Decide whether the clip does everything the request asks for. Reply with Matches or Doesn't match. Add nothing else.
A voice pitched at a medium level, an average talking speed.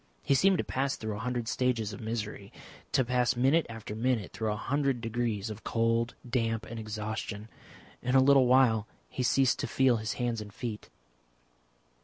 Doesn't match